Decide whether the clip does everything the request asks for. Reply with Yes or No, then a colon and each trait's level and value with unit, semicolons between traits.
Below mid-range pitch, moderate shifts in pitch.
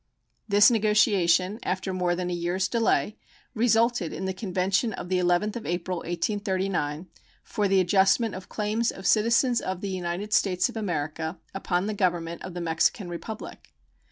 No: high, 190 Hz; average, 3.1 semitones